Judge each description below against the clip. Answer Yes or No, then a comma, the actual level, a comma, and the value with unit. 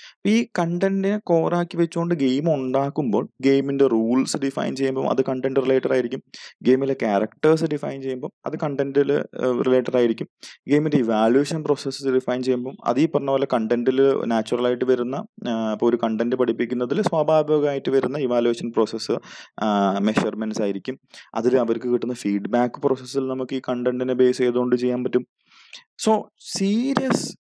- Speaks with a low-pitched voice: Yes, low, 130 Hz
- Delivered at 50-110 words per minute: No, fast, 125 wpm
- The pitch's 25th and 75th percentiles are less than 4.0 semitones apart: Yes, average, 2.8 semitones